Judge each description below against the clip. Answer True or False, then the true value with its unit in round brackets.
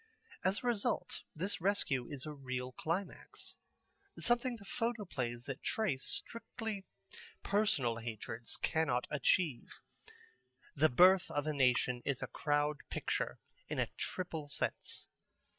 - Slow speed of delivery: True (125 wpm)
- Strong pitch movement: True (7.7 semitones)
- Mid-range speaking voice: True (150 Hz)